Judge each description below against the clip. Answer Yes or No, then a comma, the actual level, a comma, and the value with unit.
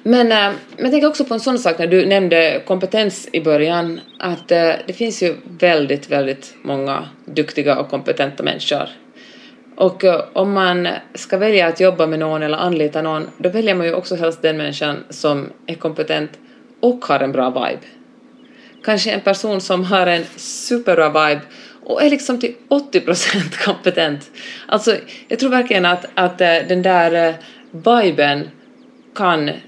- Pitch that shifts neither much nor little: No, wide, 6.6 semitones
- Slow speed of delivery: No, average, 160 wpm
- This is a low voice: No, medium, 180 Hz